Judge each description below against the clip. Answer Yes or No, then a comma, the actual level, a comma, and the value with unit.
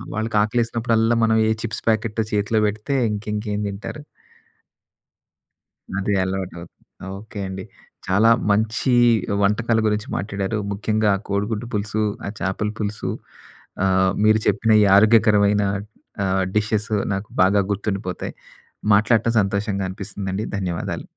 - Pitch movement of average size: No, narrow, 1.8 semitones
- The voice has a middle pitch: No, low, 105 Hz